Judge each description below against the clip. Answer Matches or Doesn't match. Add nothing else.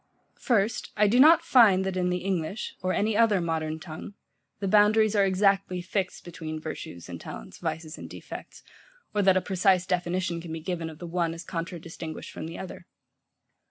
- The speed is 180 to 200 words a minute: Matches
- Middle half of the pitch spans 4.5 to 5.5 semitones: Doesn't match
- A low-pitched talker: Doesn't match